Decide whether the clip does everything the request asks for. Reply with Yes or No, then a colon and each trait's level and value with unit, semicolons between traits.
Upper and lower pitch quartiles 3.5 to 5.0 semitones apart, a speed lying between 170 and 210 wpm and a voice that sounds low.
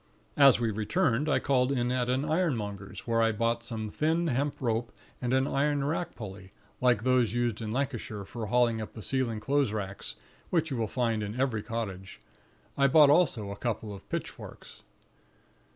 Yes: average, 4.0 semitones; average, 180 wpm; low, 120 Hz